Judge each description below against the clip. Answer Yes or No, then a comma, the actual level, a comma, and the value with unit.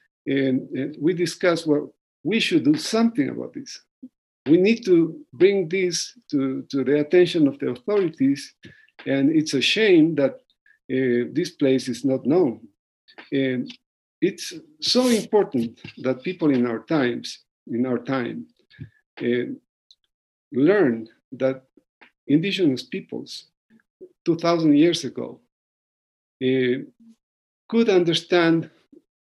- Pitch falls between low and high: Yes, medium, 170 Hz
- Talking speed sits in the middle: No, slow, 115 wpm